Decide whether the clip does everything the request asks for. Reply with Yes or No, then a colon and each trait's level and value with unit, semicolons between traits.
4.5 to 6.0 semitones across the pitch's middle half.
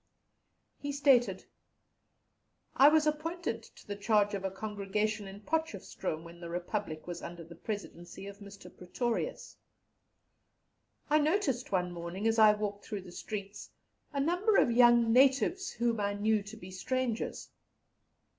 Yes: average, 4.9 semitones